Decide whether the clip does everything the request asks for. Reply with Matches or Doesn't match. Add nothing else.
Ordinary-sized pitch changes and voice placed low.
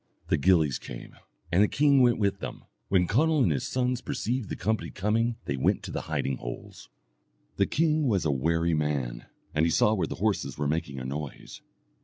Doesn't match